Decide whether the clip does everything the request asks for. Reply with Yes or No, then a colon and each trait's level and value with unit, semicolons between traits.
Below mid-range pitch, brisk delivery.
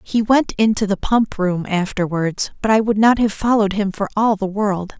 No: high, 205 Hz; fast, 215 wpm